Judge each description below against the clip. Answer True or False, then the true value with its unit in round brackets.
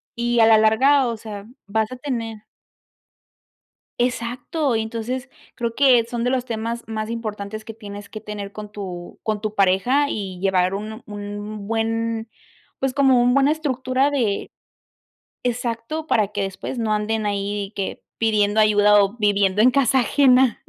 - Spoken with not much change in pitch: False (3.1 semitones)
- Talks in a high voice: True (225 Hz)